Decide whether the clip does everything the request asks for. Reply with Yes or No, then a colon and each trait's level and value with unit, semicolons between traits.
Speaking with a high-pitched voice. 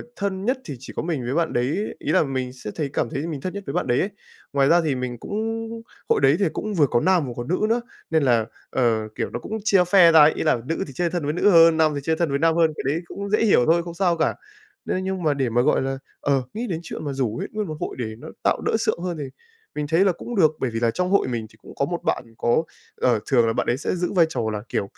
No: medium, 155 Hz